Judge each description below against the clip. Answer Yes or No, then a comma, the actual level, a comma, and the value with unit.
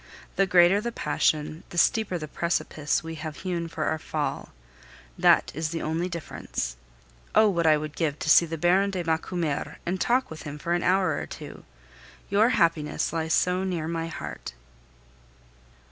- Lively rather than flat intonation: No, average, 2.7 semitones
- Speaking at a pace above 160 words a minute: Yes, average, 175 wpm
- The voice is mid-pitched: Yes, medium, 165 Hz